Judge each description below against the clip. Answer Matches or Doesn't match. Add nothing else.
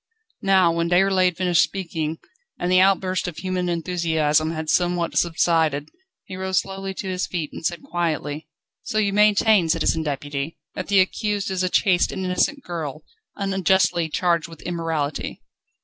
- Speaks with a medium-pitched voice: Matches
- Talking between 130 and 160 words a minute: Matches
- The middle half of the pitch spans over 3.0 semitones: Doesn't match